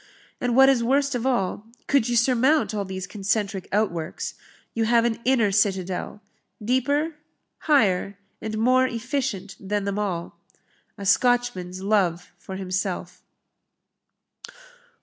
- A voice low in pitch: No, high, 215 Hz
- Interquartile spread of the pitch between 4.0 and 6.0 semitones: Yes, average, 4.5 semitones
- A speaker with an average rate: No, slow, 125 wpm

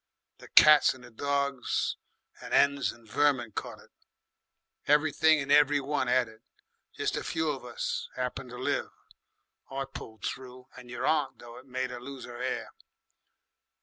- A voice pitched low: Yes, low, 130 Hz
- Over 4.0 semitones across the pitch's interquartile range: No, narrow, 2.4 semitones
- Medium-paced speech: Yes, average, 160 wpm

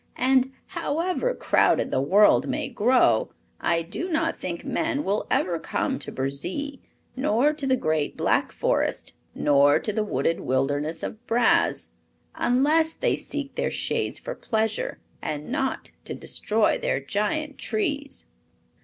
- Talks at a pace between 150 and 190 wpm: No, average, 140 wpm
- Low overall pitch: No, high, 240 Hz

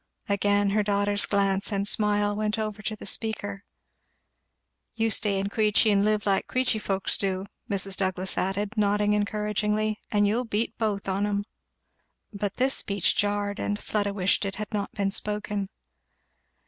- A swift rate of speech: No, average, 160 wpm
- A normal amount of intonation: No, narrow, 1.1 semitones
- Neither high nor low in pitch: No, high, 205 Hz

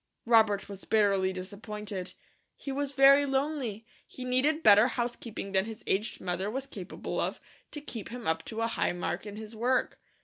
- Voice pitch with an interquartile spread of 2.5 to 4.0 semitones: No, average, 4.4 semitones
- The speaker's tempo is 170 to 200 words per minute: Yes, average, 175 wpm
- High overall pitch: Yes, high, 220 Hz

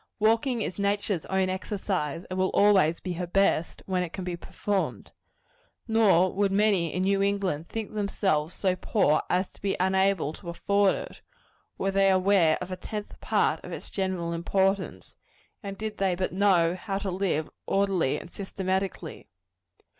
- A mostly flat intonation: Yes, narrow, 1.8 semitones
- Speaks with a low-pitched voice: No, high, 190 Hz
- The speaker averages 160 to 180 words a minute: Yes, average, 165 wpm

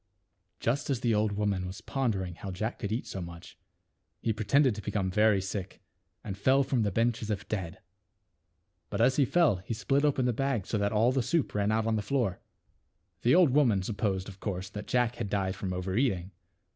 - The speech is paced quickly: Yes, fast, 215 wpm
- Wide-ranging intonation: No, average, 4.1 semitones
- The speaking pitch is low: Yes, low, 105 Hz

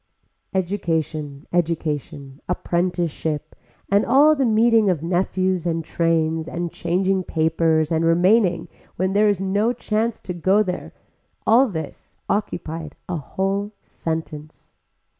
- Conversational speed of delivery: No, slow, 120 wpm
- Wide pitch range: No, average, 3.8 semitones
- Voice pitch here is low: No, medium, 175 Hz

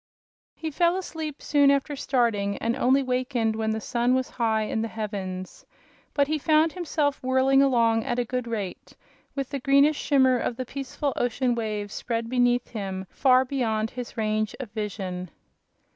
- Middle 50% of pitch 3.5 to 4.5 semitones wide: Yes, average, 3.9 semitones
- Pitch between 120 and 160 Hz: No, high, 245 Hz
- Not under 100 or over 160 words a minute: No, average, 170 wpm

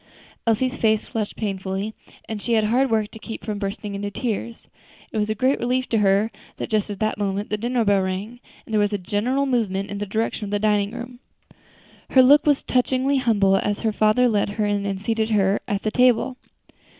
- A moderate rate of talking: No, fast, 215 wpm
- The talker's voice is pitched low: No, high, 215 Hz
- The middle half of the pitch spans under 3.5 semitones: Yes, average, 2.8 semitones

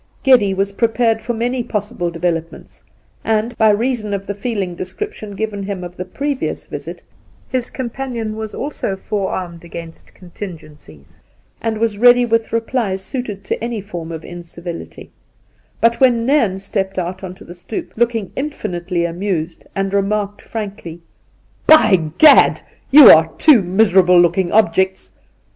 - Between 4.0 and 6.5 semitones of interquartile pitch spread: Yes, average, 4.4 semitones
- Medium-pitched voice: No, high, 200 Hz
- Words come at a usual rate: Yes, average, 155 wpm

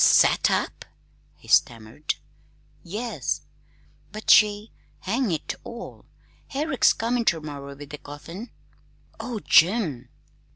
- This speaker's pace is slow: Yes, slow, 115 wpm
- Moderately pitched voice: No, high, 195 Hz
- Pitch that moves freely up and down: Yes, wide, 7.9 semitones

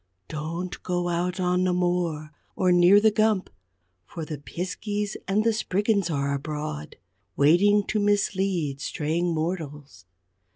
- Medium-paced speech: No, slow, 130 wpm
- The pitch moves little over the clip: No, average, 4.3 semitones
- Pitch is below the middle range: No, medium, 180 Hz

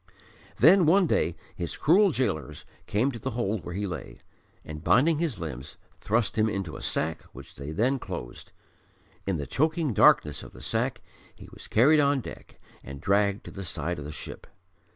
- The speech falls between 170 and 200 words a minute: Yes, average, 185 wpm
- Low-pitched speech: Yes, low, 105 Hz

